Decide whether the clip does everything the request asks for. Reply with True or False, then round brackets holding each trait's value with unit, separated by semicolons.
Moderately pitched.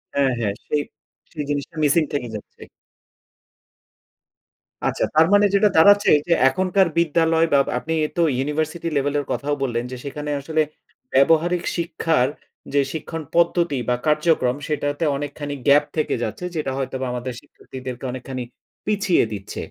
True (150 Hz)